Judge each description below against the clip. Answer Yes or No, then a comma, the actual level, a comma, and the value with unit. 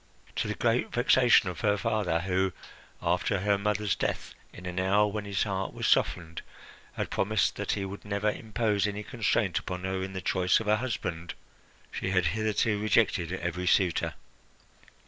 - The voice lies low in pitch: Yes, low, 100 Hz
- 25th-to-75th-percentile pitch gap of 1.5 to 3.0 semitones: Yes, narrow, 2.5 semitones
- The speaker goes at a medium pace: Yes, average, 170 wpm